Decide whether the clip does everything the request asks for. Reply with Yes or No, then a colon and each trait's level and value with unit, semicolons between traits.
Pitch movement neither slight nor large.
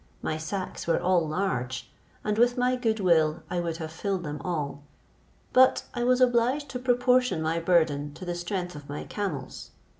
No: wide, 7.2 semitones